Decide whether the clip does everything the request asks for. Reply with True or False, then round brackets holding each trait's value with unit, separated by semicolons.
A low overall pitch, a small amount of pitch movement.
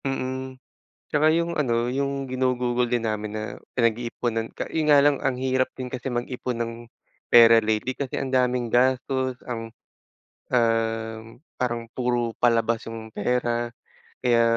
True (120 Hz; 2.1 semitones)